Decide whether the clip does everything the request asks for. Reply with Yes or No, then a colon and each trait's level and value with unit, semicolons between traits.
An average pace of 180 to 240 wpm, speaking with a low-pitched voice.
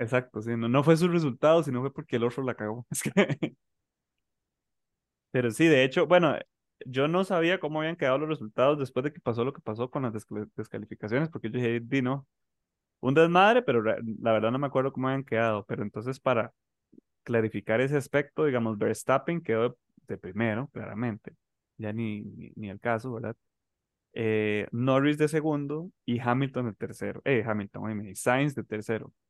Yes: average, 185 wpm; low, 125 Hz